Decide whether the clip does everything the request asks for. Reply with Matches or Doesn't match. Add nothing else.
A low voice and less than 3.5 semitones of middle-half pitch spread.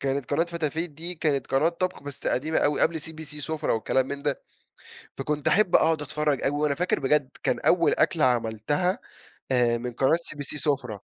Doesn't match